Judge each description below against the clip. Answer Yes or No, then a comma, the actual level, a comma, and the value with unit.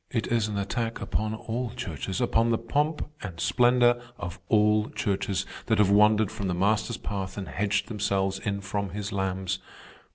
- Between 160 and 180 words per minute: Yes, average, 170 wpm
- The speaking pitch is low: Yes, low, 105 Hz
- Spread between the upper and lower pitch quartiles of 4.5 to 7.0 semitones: No, average, 2.8 semitones